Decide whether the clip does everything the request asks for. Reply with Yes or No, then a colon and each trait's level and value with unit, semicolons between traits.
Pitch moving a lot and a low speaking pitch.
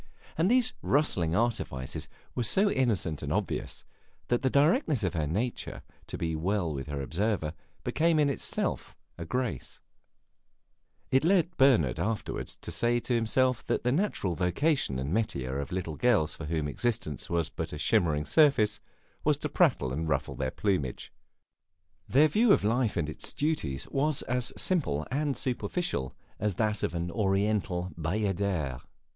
Yes: wide, 8.6 semitones; low, 105 Hz